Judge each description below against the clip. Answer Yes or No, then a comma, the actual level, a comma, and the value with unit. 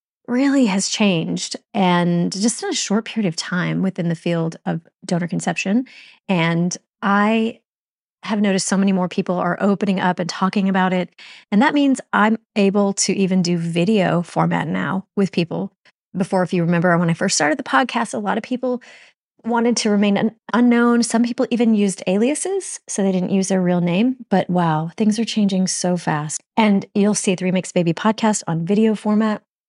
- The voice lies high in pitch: Yes, high, 195 Hz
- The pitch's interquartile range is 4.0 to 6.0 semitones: No, average, 3.5 semitones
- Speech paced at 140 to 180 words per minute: No, average, 190 wpm